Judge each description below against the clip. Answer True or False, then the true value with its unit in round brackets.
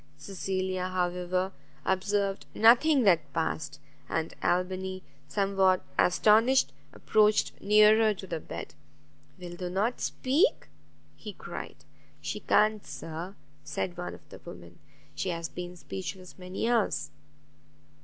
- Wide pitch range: False (2.9 semitones)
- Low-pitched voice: False (190 Hz)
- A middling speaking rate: False (115 wpm)